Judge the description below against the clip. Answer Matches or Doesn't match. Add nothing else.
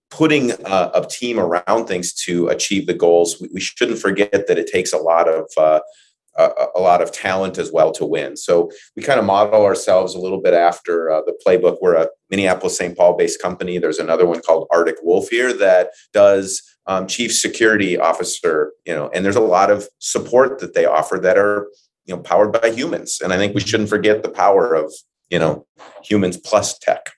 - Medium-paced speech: Doesn't match